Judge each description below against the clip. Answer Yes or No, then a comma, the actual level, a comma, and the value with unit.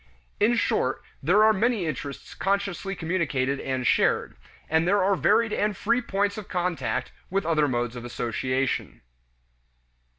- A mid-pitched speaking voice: Yes, medium, 175 Hz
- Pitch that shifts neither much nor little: No, wide, 7.1 semitones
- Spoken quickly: No, average, 140 wpm